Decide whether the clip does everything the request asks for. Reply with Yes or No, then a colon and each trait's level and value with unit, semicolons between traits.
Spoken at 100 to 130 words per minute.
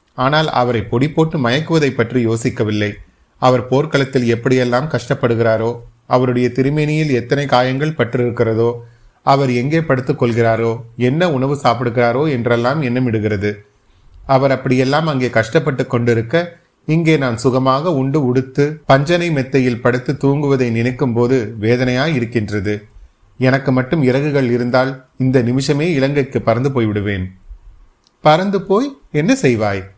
Yes: average, 110 wpm